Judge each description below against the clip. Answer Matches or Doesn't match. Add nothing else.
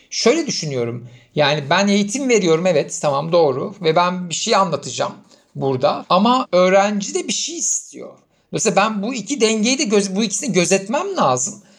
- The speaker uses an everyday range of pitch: Matches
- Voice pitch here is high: Matches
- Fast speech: Matches